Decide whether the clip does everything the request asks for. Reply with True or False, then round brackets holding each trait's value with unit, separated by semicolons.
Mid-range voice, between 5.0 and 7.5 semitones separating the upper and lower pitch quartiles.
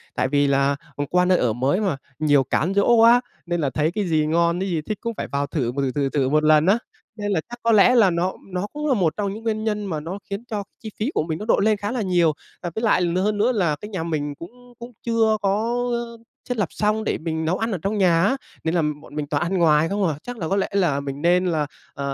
True (180 Hz; 5.6 semitones)